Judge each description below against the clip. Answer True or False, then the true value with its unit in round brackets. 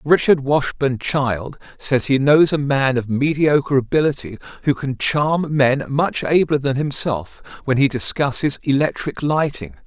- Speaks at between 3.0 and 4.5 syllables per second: True (4.3 syllables/s)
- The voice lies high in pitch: False (135 Hz)